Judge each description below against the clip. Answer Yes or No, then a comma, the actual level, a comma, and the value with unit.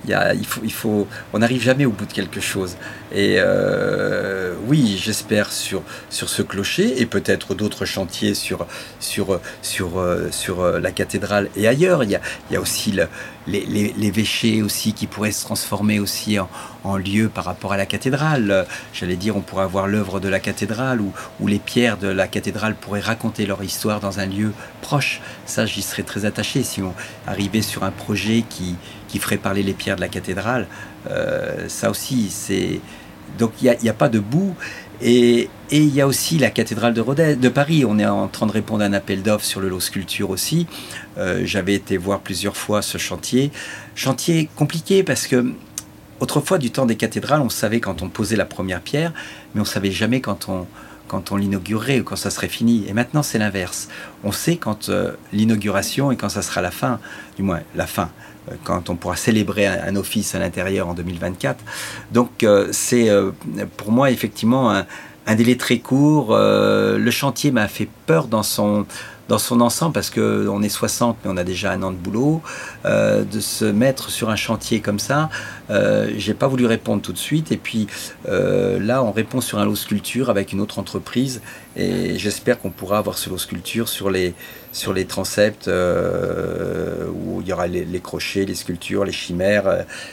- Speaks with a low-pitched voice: Yes, low, 105 Hz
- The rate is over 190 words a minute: Yes, average, 200 wpm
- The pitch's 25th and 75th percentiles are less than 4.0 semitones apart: Yes, average, 3.3 semitones